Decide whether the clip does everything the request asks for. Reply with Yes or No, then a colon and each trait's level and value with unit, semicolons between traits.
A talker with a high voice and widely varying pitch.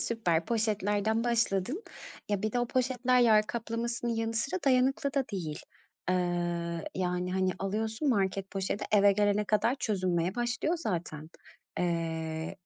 No: high, 210 Hz; average, 4.1 semitones